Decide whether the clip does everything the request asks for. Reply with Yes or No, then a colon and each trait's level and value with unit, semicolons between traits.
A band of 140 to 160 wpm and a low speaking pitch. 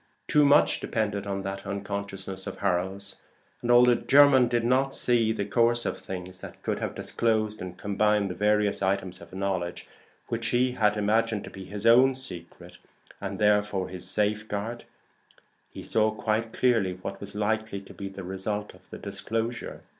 No: average, 170 wpm; low, 105 Hz